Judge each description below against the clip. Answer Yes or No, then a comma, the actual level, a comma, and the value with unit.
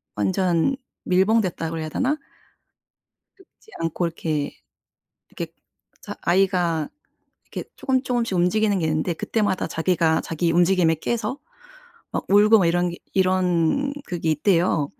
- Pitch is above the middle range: No, medium, 180 Hz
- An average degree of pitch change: Yes, average, 3.8 semitones